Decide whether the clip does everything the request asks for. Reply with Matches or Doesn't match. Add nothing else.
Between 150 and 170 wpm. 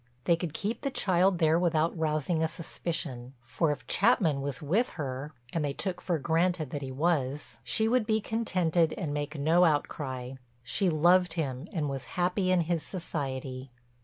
Matches